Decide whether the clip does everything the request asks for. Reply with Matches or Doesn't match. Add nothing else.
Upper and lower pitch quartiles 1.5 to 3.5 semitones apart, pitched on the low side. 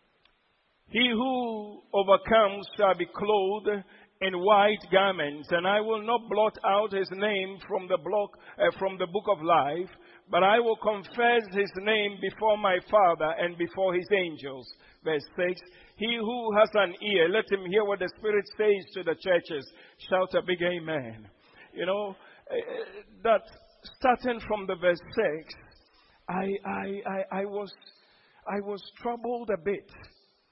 Doesn't match